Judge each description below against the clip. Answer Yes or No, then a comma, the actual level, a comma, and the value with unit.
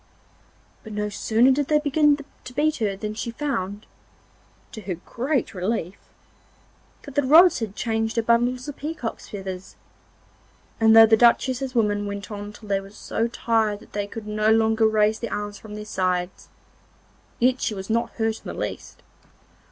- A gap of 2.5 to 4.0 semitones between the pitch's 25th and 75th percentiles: Yes, average, 2.8 semitones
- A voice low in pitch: No, high, 220 Hz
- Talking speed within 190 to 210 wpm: No, average, 175 wpm